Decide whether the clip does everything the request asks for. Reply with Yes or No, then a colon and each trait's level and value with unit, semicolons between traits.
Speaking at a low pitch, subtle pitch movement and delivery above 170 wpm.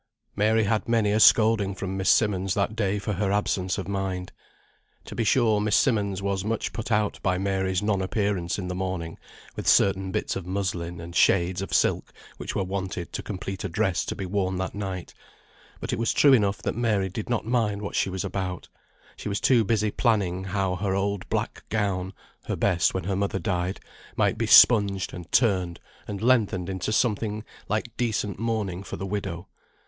Yes: low, 100 Hz; narrow, 2.2 semitones; average, 195 wpm